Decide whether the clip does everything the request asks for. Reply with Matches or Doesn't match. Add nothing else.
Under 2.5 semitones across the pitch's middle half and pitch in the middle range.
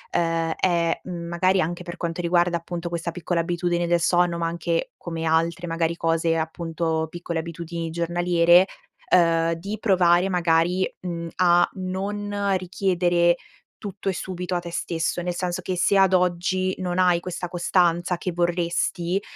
Matches